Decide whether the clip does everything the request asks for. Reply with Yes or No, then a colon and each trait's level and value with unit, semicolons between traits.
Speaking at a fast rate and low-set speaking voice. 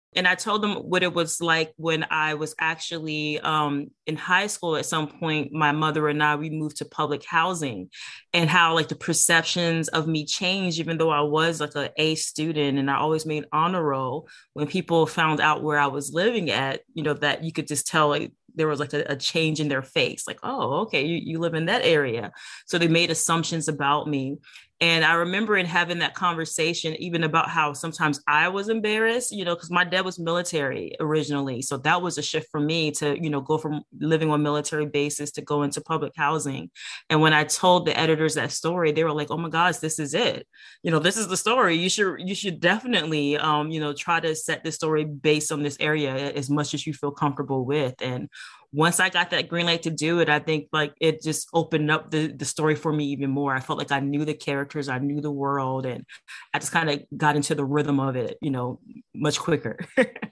No: fast, 230 wpm; medium, 155 Hz